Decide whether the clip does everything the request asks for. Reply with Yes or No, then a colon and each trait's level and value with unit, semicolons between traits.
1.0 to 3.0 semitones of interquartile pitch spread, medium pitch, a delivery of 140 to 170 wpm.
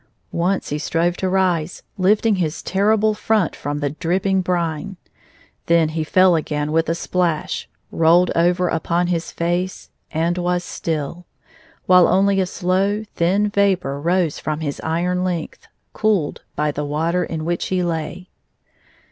Yes: narrow, 2.5 semitones; medium, 175 Hz; average, 145 wpm